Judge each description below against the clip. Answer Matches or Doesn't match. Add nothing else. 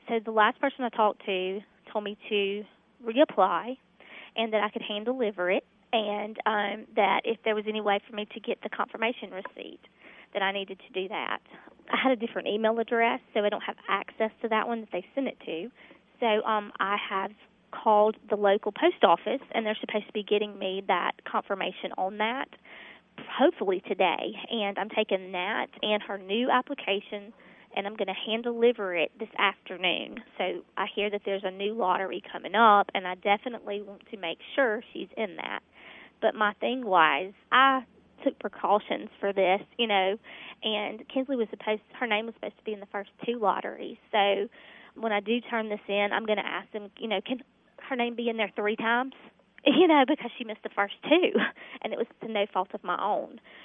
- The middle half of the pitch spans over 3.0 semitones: Doesn't match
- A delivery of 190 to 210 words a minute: Matches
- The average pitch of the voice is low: Doesn't match